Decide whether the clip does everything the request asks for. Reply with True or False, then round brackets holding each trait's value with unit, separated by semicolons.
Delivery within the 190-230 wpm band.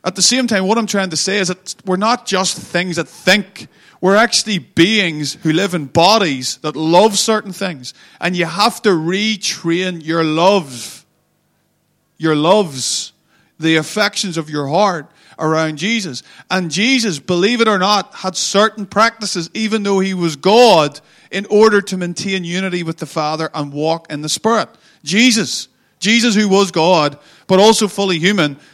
False (165 wpm)